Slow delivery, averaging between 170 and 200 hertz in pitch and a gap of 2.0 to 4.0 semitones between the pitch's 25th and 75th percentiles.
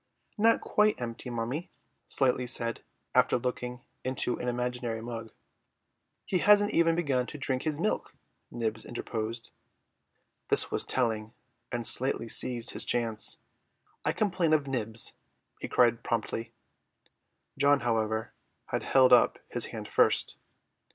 No: slow, 130 wpm; low, 125 Hz; average, 3.5 semitones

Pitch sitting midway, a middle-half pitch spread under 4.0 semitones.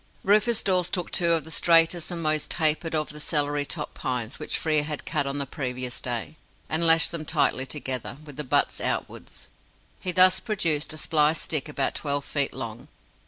Yes: medium, 155 Hz; average, 2.7 semitones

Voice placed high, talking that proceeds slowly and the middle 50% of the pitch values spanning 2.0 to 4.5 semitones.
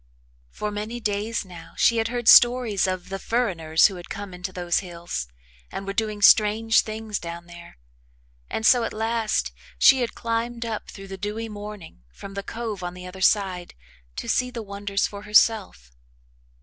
No: high, 205 Hz; average, 175 wpm; average, 3.6 semitones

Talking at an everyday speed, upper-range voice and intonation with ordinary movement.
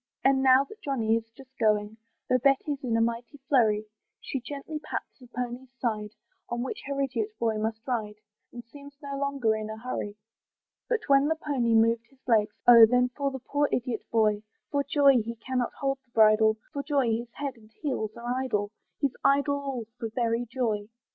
Yes: average, 195 wpm; high, 245 Hz; average, 3.6 semitones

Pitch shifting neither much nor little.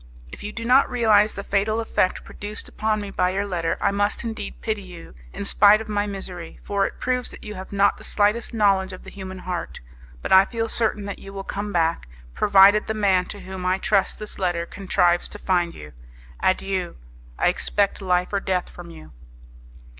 No: narrow, 2.3 semitones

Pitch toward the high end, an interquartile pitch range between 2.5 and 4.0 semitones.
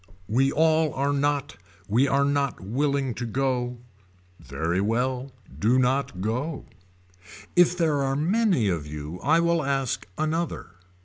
No: low, 135 Hz; average, 3.7 semitones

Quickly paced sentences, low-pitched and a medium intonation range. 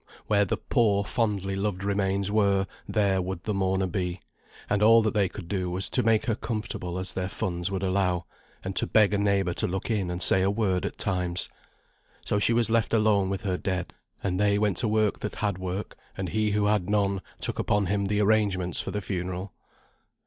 No: fast, 215 wpm; low, 100 Hz; narrow, 2.1 semitones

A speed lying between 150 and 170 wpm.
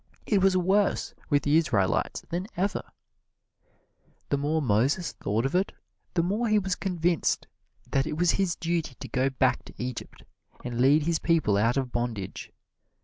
Yes: average, 165 wpm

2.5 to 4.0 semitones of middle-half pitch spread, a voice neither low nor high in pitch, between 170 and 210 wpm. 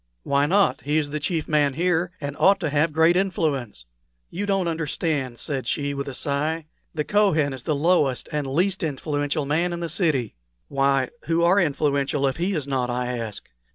Yes: average, 3.4 semitones; medium, 150 Hz; average, 190 wpm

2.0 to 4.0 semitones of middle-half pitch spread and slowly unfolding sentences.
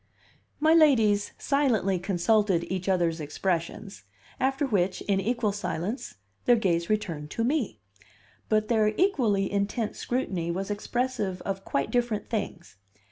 No: average, 4.6 semitones; slow, 130 wpm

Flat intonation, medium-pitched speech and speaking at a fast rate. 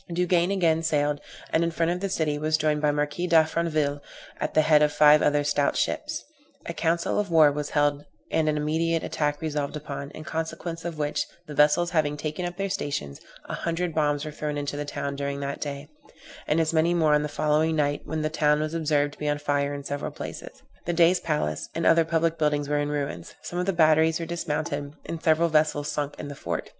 Yes: narrow, 2.0 semitones; medium, 155 Hz; fast, 225 wpm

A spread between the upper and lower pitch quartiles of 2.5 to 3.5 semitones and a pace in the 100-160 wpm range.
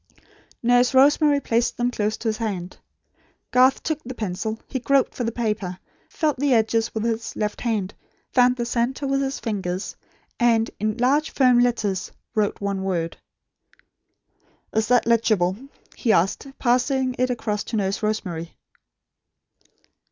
Yes: average, 3.2 semitones; average, 150 wpm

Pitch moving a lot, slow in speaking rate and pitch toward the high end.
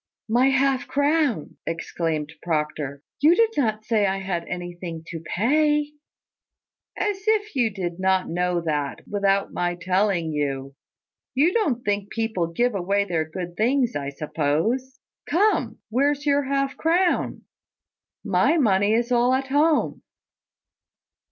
Yes: wide, 8.1 semitones; slow, 130 wpm; high, 210 Hz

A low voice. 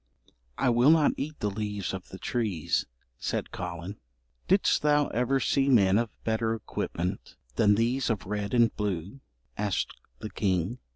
Yes: low, 110 Hz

